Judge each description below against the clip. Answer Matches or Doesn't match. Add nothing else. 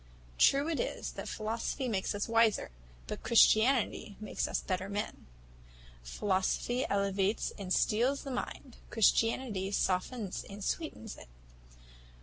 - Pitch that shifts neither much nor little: Matches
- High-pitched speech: Matches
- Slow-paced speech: Matches